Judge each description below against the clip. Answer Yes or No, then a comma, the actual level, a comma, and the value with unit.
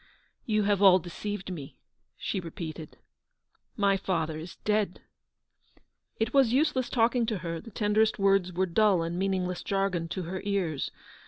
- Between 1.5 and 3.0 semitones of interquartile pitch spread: No, average, 3.4 semitones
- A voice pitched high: Yes, high, 195 Hz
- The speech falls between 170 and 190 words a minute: No, average, 155 wpm